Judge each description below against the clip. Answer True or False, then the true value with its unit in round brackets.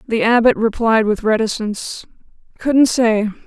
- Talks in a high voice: True (225 Hz)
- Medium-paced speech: False (120 wpm)